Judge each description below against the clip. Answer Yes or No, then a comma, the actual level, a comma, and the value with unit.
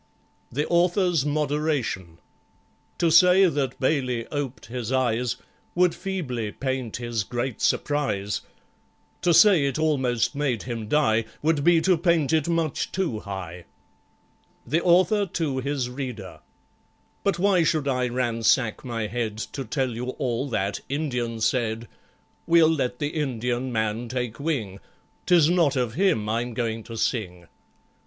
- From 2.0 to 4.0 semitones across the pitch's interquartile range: No, wide, 5.4 semitones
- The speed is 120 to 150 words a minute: Yes, average, 140 wpm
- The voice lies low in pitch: Yes, low, 130 Hz